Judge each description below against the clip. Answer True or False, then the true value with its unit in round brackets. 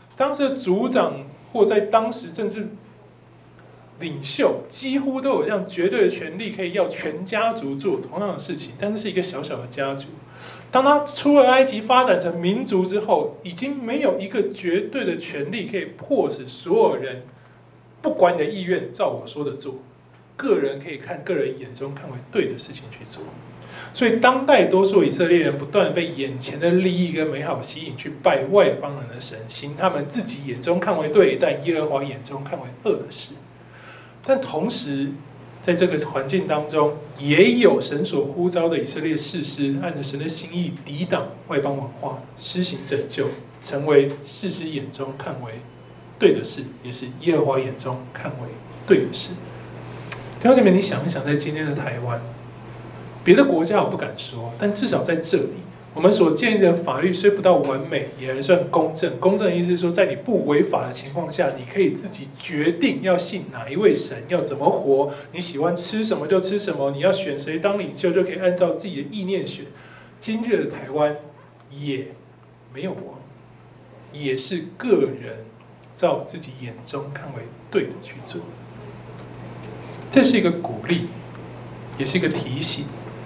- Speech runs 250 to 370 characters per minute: True (260 characters per minute)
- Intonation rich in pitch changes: True (5.8 semitones)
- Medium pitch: True (160 Hz)